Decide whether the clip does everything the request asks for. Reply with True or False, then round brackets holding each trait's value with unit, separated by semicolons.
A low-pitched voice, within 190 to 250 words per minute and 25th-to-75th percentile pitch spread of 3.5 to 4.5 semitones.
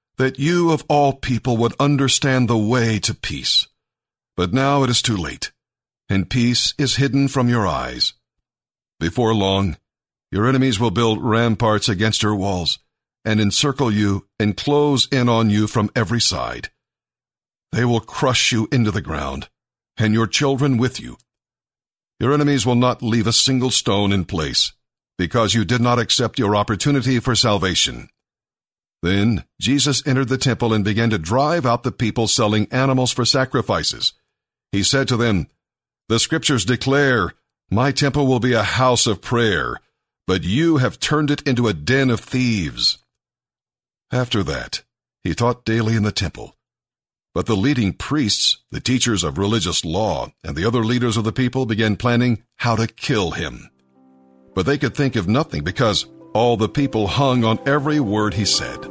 False (115 Hz; 165 wpm; 3.8 semitones)